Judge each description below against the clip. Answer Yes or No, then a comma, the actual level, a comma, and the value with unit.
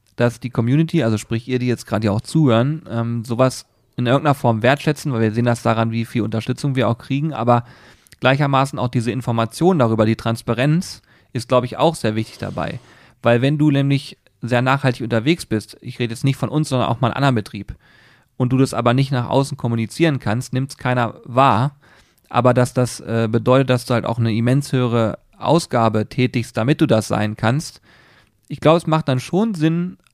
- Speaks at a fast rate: Yes, fast, 205 wpm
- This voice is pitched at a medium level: No, low, 125 Hz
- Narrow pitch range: No, average, 3.0 semitones